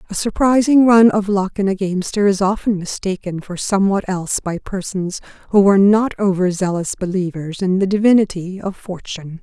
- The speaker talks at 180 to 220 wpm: No, average, 170 wpm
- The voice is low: No, high, 195 Hz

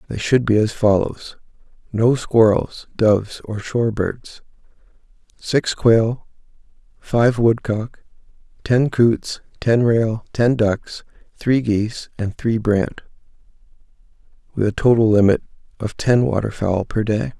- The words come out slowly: Yes, slow, 120 wpm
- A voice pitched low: Yes, low, 110 Hz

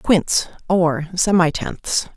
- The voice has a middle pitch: Yes, medium, 175 Hz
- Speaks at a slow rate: Yes, slow, 85 wpm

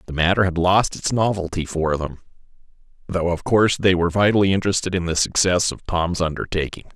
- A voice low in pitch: Yes, very low, 90 Hz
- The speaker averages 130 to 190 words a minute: Yes, average, 180 wpm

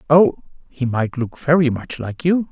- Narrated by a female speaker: No, male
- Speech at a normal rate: Yes, average, 190 wpm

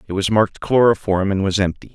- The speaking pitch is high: No, low, 100 Hz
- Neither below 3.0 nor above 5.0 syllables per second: No, 6.2 syllables/s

